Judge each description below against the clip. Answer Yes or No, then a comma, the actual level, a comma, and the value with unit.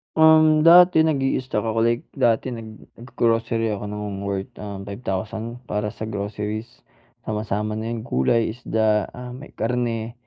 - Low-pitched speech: Yes, low, 115 Hz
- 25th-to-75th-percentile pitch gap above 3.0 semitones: No, average, 2.7 semitones